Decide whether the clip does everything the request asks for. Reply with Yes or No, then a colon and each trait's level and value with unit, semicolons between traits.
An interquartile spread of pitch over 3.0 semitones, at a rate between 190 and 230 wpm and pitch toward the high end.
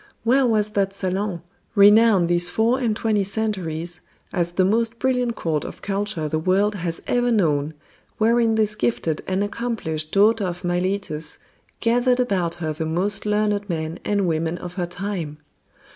No: average, 4.2 semitones; average, 160 wpm; high, 195 Hz